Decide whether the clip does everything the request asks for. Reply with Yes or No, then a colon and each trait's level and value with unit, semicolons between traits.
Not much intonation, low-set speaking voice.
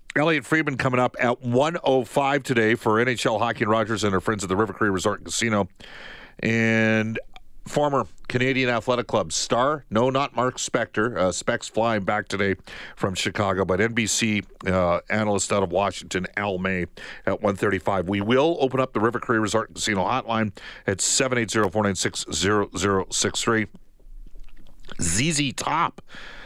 No: average, 3.8 semitones; low, 110 Hz